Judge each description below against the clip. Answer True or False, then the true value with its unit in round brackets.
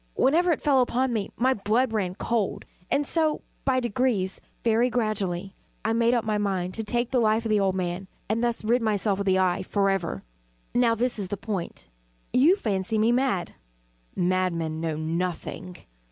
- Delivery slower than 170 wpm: False (180 wpm)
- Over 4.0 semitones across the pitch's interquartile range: True (4.4 semitones)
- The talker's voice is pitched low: False (215 Hz)